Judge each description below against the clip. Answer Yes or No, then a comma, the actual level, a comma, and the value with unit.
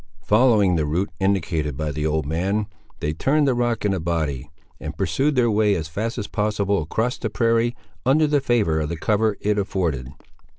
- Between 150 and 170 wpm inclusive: No, average, 195 wpm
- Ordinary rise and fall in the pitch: No, wide, 6.4 semitones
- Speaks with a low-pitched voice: Yes, low, 100 Hz